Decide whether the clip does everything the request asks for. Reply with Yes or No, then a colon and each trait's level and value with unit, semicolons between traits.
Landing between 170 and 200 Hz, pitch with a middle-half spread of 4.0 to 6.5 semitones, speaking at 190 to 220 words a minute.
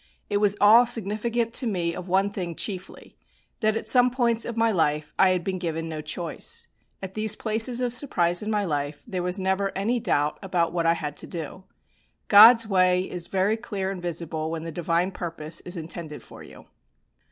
Yes: high, 190 Hz; average, 4.4 semitones; average, 200 wpm